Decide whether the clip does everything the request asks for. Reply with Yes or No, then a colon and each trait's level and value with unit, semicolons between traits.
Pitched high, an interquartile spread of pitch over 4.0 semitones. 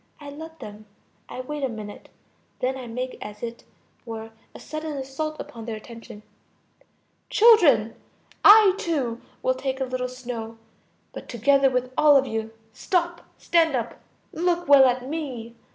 Yes: very high, 255 Hz; average, 4.6 semitones